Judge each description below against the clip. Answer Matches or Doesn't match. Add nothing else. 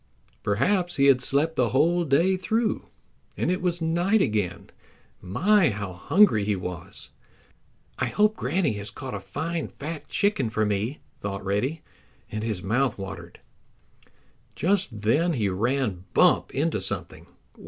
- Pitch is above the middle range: Doesn't match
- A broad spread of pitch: Matches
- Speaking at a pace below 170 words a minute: Matches